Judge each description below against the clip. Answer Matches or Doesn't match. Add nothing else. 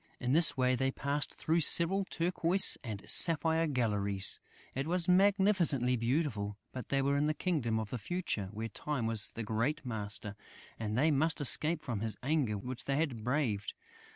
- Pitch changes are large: Matches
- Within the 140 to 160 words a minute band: Doesn't match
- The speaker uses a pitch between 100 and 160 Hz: Matches